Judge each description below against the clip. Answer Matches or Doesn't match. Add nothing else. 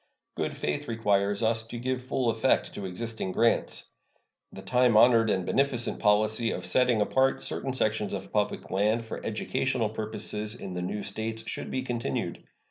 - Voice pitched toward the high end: Doesn't match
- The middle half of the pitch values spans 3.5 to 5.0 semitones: Doesn't match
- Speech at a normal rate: Matches